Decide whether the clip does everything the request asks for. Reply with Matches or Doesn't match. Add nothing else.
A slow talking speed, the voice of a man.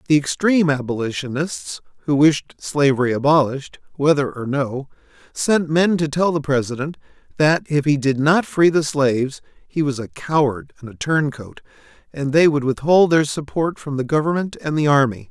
Doesn't match